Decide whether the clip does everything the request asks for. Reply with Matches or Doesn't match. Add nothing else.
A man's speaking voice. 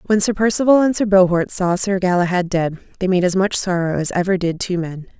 Doesn't match